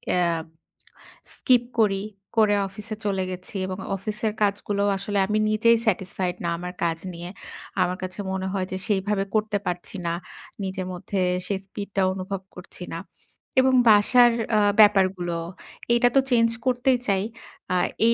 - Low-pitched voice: No, high, 200 Hz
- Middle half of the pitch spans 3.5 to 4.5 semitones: No, narrow, 2.5 semitones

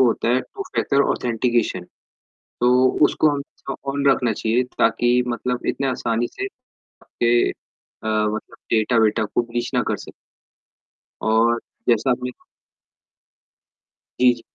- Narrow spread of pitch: Yes, narrow, 1.9 semitones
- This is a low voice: Yes, low, 120 Hz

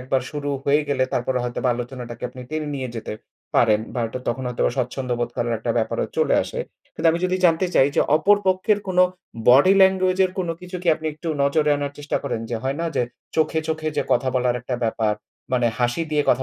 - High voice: No, low, 135 Hz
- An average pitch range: Yes, average, 4.7 semitones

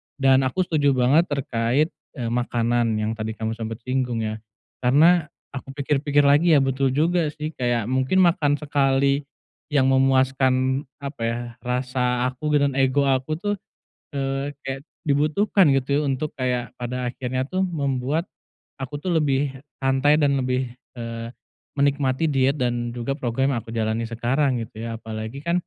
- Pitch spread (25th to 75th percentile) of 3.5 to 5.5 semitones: No, average, 2.7 semitones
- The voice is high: No, low, 135 Hz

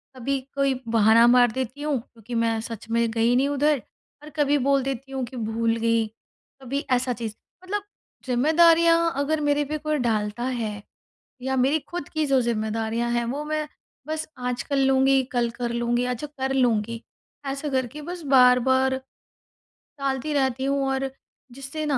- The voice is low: No, very high, 260 Hz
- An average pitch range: Yes, average, 3.2 semitones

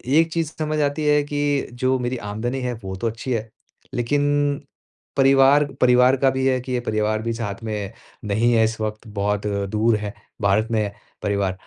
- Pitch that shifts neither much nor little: Yes, average, 4.1 semitones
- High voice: No, low, 120 Hz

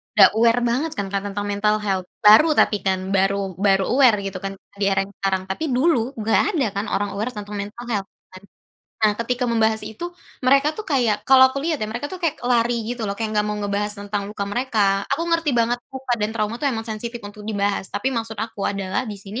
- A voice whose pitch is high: Yes, high, 215 Hz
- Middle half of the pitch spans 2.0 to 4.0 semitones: Yes, average, 3.4 semitones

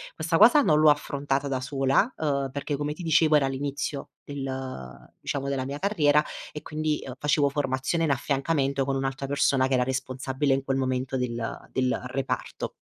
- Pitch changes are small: Yes, narrow, 1.9 semitones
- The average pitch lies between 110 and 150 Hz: Yes, medium, 140 Hz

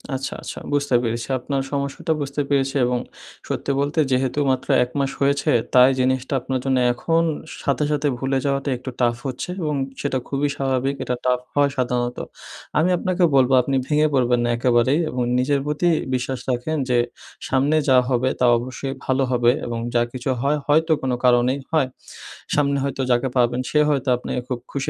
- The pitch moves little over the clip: Yes, narrow, 2.2 semitones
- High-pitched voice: No, low, 135 Hz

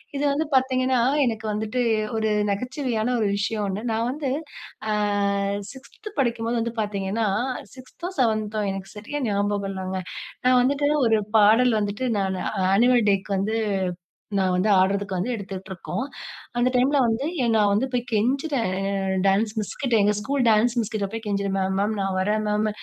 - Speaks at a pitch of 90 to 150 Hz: No, high, 220 Hz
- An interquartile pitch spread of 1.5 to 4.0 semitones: Yes, average, 3.7 semitones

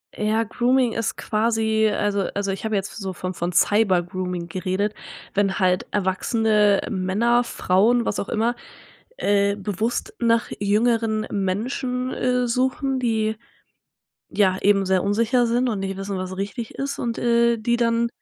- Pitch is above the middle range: Yes, high, 215 Hz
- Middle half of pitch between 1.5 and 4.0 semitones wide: Yes, average, 3.2 semitones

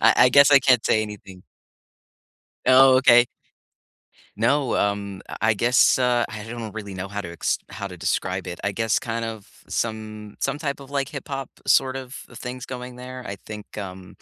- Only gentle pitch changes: No, average, 4.0 semitones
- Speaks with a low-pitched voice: Yes, low, 115 Hz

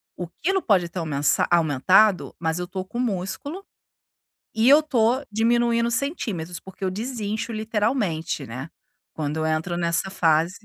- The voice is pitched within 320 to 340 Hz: No, high, 190 Hz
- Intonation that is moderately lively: No, wide, 5.8 semitones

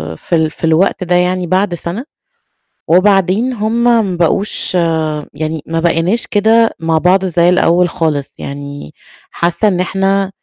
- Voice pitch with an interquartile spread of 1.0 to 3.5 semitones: Yes, average, 3.1 semitones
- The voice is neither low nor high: Yes, medium, 180 Hz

